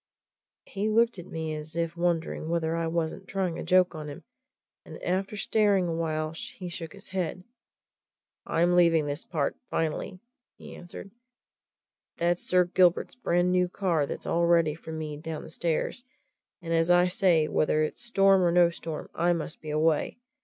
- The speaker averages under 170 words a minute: No, average, 175 wpm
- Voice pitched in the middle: Yes, medium, 170 Hz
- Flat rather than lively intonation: Yes, narrow, 2.2 semitones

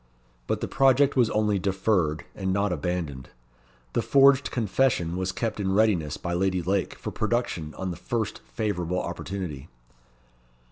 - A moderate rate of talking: Yes, average, 145 wpm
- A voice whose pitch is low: Yes, very low, 95 Hz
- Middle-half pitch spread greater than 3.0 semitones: Yes, average, 4.0 semitones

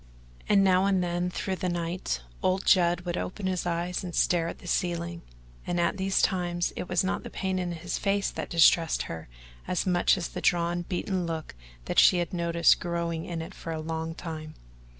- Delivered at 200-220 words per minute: Yes, fast, 205 wpm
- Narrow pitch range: Yes, narrow, 1.5 semitones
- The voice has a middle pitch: Yes, medium, 175 Hz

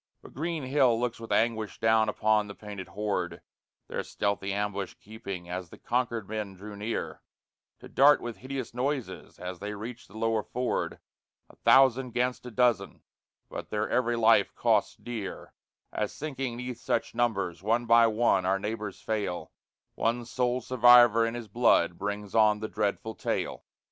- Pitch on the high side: No, low, 110 Hz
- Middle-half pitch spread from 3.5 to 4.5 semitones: No, average, 2.9 semitones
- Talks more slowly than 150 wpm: No, average, 165 wpm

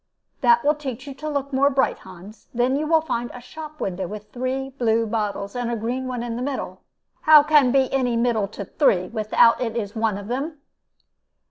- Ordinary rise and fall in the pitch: Yes, average, 3.7 semitones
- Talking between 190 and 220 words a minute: Yes, fast, 205 wpm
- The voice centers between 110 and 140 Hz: No, high, 245 Hz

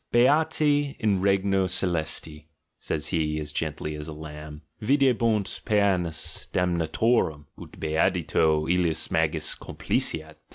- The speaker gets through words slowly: Yes, slow, 110 wpm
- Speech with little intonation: No, average, 5.0 semitones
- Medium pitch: No, very low, 85 Hz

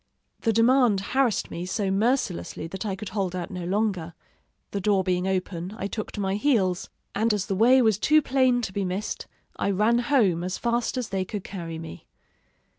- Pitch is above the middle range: Yes, high, 200 Hz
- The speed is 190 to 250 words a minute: Yes, average, 195 wpm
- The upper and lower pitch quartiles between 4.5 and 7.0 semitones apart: No, average, 3.9 semitones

